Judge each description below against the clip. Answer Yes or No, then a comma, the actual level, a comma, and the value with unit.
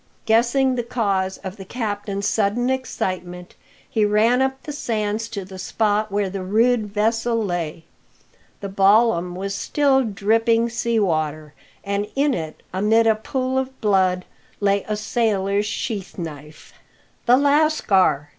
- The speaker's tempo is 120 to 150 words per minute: Yes, average, 140 wpm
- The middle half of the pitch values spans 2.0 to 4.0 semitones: Yes, average, 3.6 semitones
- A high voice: Yes, high, 210 Hz